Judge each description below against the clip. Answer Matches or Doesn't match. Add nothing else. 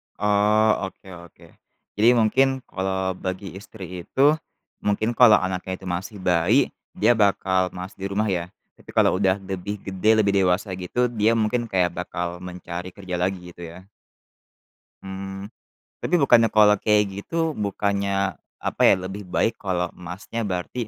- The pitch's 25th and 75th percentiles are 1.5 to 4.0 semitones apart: Matches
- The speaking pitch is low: Matches